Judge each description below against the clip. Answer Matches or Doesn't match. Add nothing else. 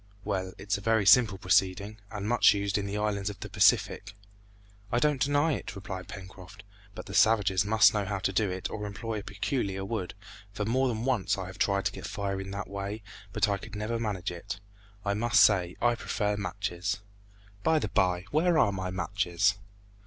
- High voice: Doesn't match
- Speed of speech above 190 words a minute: Matches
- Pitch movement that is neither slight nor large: Doesn't match